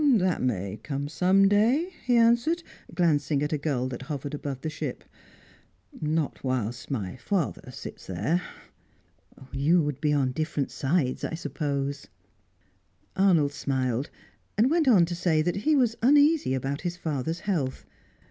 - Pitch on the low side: No, medium, 155 Hz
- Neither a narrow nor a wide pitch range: No, wide, 5.8 semitones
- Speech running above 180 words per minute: No, average, 145 wpm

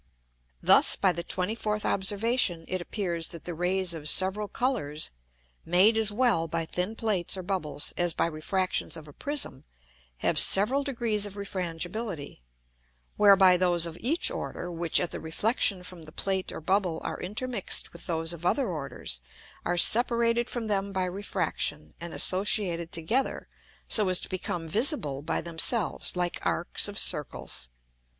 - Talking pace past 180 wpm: No, average, 155 wpm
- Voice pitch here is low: No, medium, 185 Hz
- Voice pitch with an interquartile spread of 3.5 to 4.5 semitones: Yes, average, 4.1 semitones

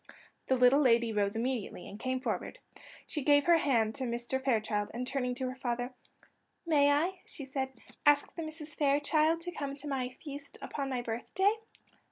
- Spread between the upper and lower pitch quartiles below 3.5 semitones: Yes, average, 3.1 semitones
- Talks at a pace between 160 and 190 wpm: Yes, average, 180 wpm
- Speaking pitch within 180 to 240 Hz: No, very high, 265 Hz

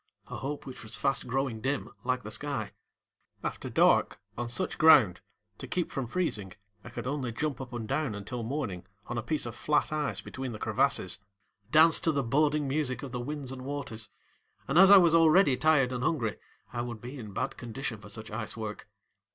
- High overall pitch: No, low, 130 Hz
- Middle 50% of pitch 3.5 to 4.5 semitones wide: Yes, average, 4.2 semitones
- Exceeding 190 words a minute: Yes, average, 200 wpm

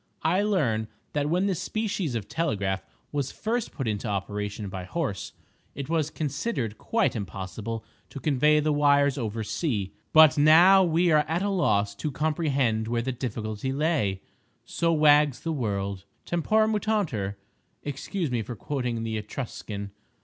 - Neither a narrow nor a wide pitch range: No, wide, 7.0 semitones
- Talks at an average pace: Yes, average, 150 wpm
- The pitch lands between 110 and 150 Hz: Yes, medium, 140 Hz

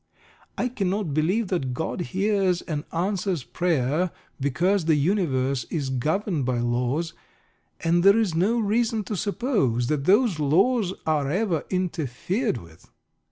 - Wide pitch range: Yes, wide, 6.1 semitones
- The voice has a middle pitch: Yes, medium, 175 Hz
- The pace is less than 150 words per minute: Yes, slow, 135 wpm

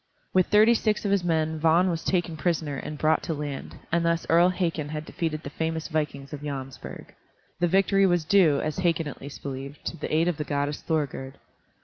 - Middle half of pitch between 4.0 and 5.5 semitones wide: No, average, 3.0 semitones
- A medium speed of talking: No, fast, 210 wpm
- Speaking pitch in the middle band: Yes, medium, 160 Hz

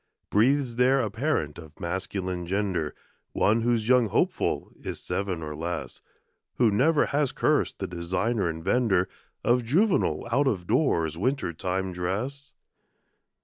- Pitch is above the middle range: No, low, 105 Hz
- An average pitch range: No, wide, 6.3 semitones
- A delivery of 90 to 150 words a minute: Yes, average, 140 wpm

